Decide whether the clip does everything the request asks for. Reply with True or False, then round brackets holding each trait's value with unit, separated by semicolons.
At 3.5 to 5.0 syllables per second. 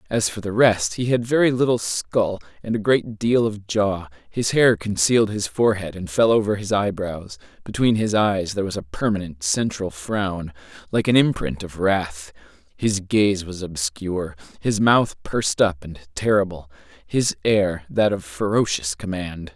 True (4.5 syllables/s)